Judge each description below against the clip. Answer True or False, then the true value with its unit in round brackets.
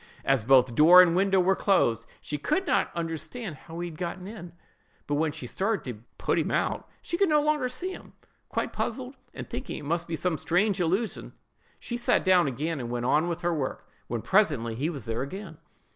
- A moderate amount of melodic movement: False (5.9 semitones)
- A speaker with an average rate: False (215 wpm)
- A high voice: False (170 Hz)